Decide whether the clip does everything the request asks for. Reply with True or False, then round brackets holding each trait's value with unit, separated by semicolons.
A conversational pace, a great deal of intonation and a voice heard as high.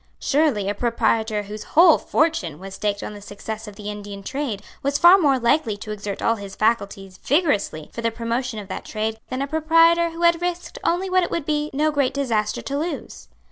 False (210 wpm; 6.9 semitones; 235 Hz)